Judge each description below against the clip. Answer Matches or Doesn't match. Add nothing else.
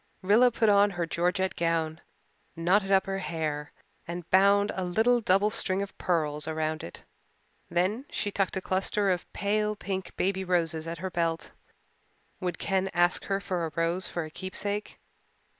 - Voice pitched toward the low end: Doesn't match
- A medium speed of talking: Matches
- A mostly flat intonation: Doesn't match